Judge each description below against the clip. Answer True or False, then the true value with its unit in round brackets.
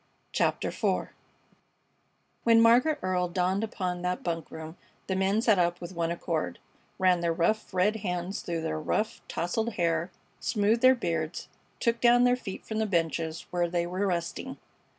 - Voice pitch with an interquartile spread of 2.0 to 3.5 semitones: False (4.3 semitones)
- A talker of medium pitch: True (180 Hz)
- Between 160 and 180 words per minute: True (165 wpm)